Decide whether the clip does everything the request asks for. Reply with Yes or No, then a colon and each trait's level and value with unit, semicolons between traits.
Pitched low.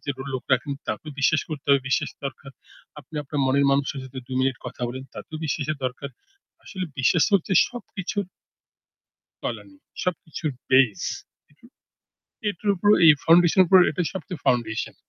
No: medium, 145 Hz